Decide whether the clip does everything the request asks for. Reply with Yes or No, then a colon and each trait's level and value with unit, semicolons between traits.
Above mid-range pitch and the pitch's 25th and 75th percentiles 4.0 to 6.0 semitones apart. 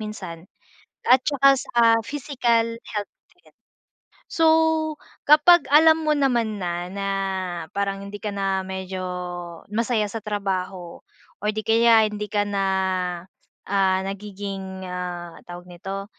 No: high, 205 Hz; average, 3.5 semitones